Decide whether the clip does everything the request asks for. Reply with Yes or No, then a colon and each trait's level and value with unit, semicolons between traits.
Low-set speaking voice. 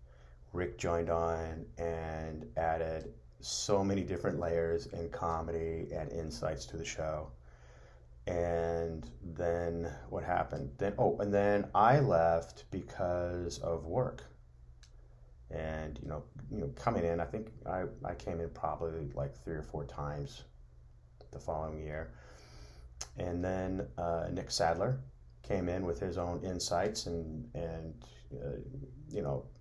Yes: very low, 80 Hz